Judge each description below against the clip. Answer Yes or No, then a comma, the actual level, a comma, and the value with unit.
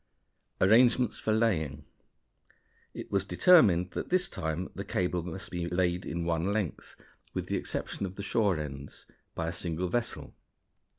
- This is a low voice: Yes, very low, 90 Hz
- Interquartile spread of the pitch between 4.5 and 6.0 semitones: No, average, 3.8 semitones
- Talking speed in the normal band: Yes, average, 155 wpm